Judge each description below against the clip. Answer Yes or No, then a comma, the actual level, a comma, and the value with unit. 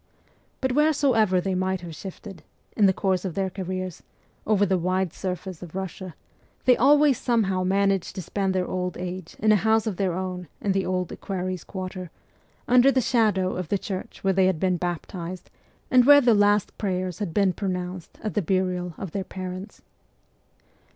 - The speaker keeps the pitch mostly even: Yes, narrow, 2.1 semitones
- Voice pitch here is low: No, high, 190 Hz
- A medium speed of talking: Yes, average, 185 wpm